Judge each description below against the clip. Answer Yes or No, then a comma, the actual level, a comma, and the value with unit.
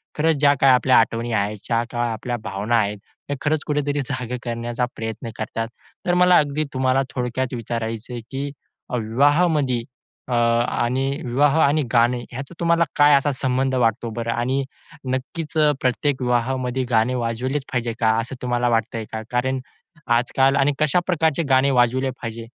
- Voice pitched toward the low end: Yes, low, 125 Hz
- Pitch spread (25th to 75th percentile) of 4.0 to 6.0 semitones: No, average, 2.9 semitones